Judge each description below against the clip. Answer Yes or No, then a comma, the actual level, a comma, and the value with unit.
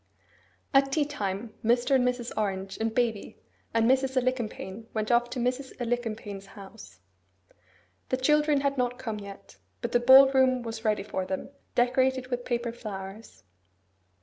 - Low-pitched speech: No, high, 240 Hz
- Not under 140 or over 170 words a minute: Yes, average, 150 wpm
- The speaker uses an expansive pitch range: No, average, 3.4 semitones